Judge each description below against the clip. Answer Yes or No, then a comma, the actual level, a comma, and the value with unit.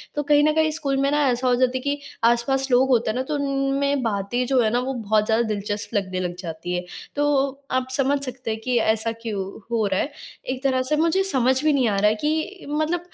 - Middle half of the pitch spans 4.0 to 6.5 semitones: Yes, average, 4.4 semitones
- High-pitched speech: Yes, very high, 255 Hz